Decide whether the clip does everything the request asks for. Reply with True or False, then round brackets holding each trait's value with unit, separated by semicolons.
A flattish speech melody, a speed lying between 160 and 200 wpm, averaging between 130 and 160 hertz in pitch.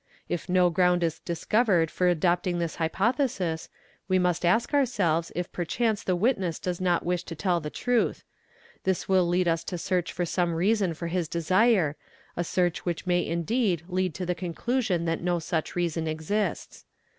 False (2.0 semitones; 175 wpm; 175 Hz)